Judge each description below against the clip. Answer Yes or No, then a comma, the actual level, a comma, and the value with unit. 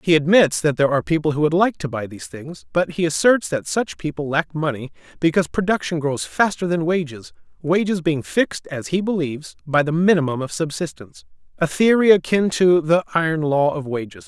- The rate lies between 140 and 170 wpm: No, average, 195 wpm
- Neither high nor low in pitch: Yes, medium, 155 Hz